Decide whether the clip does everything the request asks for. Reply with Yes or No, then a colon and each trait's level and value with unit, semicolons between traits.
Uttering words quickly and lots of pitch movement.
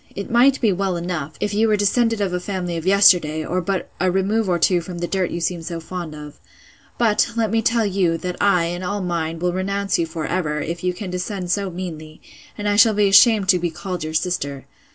No: fast, 235 wpm; average, 3.0 semitones